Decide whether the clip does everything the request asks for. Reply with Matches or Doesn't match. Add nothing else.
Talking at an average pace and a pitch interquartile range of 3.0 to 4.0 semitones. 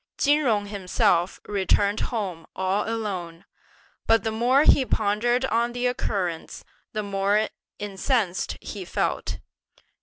Doesn't match